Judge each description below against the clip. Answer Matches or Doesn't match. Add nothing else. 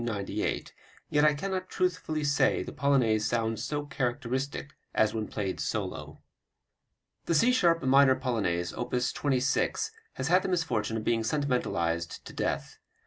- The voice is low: Matches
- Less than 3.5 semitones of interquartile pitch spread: Doesn't match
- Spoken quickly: Doesn't match